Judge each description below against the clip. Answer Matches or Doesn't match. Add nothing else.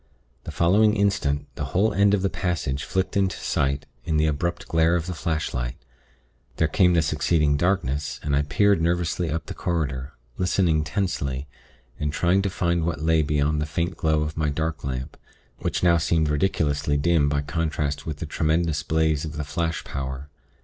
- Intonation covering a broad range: Doesn't match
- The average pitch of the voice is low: Matches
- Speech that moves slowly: Doesn't match